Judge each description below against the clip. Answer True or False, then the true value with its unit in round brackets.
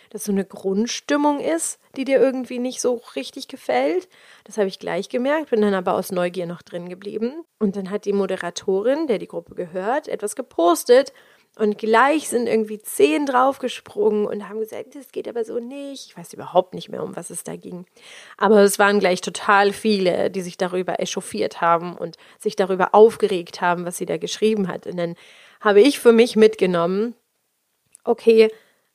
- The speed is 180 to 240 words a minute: True (185 wpm)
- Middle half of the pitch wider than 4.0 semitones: True (4.7 semitones)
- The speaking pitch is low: False (215 Hz)